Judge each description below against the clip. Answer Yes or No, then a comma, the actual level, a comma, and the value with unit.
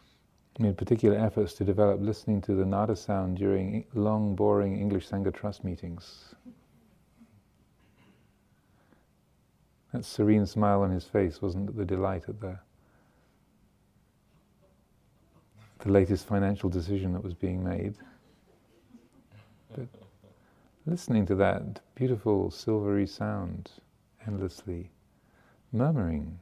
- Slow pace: Yes, slow, 100 wpm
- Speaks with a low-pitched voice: Yes, low, 100 Hz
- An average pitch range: No, narrow, 2.0 semitones